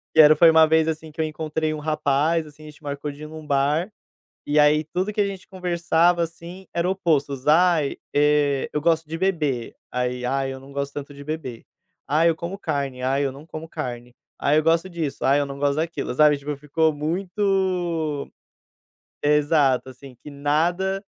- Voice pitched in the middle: Yes, medium, 155 Hz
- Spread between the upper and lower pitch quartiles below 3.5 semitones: Yes, average, 2.8 semitones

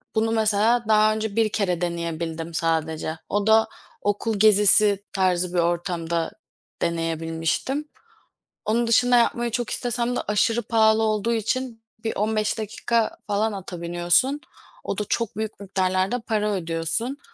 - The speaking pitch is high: Yes, high, 210 Hz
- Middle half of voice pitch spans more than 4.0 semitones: Yes, average, 4.5 semitones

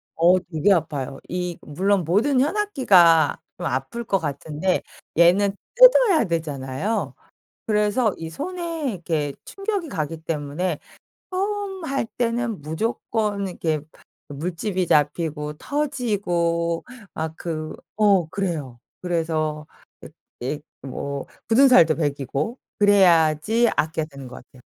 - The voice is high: No, medium, 175 Hz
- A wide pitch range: Yes, wide, 6.6 semitones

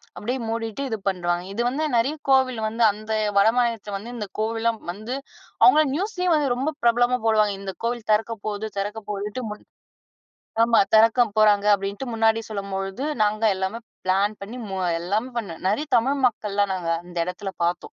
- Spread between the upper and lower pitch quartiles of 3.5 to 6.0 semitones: No, average, 3.1 semitones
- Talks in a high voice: Yes, high, 220 Hz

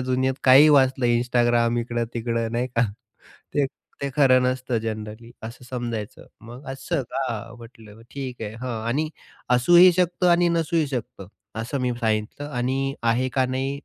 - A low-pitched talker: Yes, low, 125 Hz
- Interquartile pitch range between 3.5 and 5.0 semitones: No, average, 2.7 semitones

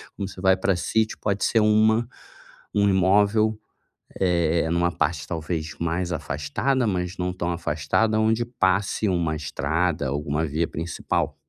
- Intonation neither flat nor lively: Yes, average, 4.2 semitones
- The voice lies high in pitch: No, very low, 90 Hz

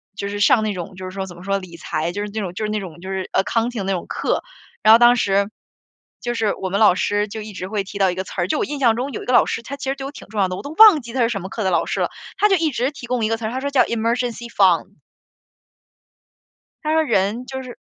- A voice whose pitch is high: Yes, high, 215 Hz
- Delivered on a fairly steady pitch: No, average, 4.3 semitones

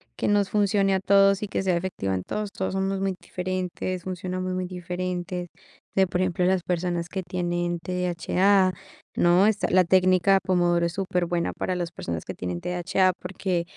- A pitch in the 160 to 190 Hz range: Yes, medium, 185 Hz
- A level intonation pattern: Yes, narrow, 1.5 semitones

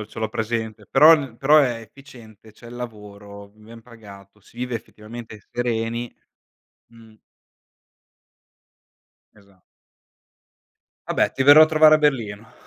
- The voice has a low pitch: Yes, low, 115 Hz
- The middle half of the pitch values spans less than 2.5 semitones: No, average, 2.8 semitones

